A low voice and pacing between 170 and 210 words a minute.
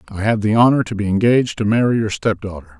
No: low, 110 Hz; fast, 235 wpm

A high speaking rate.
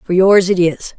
Yes: fast, 245 wpm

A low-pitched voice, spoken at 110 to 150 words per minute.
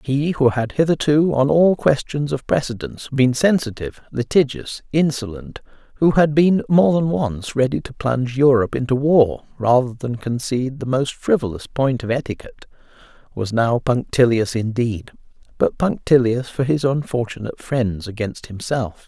Yes: low, 130 Hz; average, 145 wpm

